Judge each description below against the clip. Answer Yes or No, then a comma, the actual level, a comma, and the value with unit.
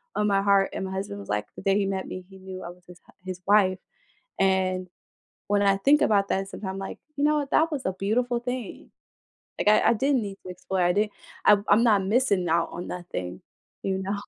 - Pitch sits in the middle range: No, high, 195 Hz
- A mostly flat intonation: Yes, narrow, 2.2 semitones